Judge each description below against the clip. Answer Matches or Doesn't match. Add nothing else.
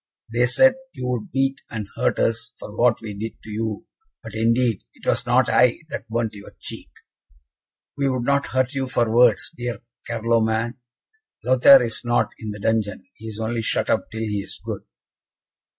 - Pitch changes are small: Matches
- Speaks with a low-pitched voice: Matches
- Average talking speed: Matches